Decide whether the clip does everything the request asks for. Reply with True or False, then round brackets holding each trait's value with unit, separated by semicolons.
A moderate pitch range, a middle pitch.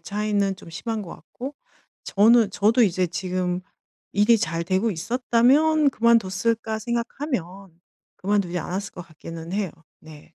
False (4.4 semitones; 200 Hz)